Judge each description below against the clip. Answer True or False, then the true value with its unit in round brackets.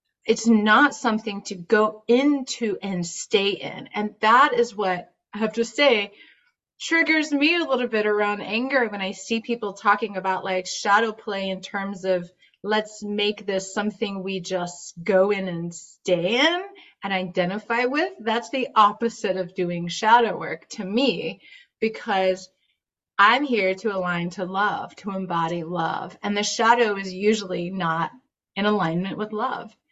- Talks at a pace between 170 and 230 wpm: False (160 wpm)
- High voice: True (210 Hz)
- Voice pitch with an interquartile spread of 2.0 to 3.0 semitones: False (3.7 semitones)